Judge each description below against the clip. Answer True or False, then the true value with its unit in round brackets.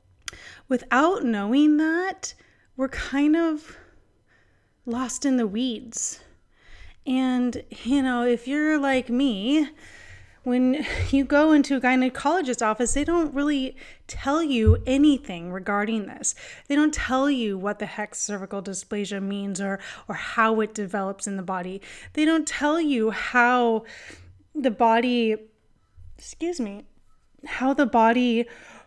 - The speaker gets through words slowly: True (130 wpm)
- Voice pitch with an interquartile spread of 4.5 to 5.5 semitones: True (5.0 semitones)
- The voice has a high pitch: True (245 Hz)